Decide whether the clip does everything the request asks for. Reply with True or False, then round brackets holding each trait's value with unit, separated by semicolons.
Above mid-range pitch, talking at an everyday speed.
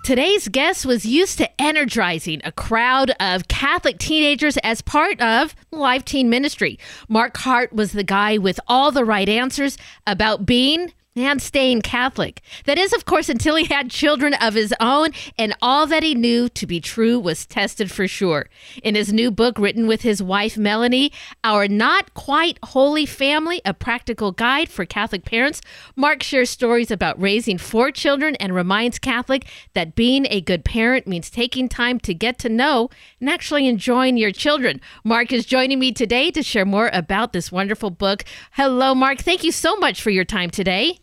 True (245 Hz; 180 wpm)